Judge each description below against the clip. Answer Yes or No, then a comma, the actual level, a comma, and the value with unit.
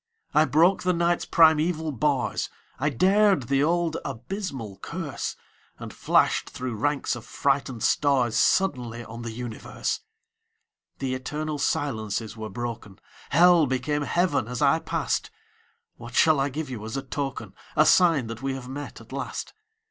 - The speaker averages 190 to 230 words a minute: No, average, 150 wpm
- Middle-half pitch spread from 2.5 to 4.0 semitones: No, average, 4.7 semitones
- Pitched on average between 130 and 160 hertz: Yes, medium, 140 Hz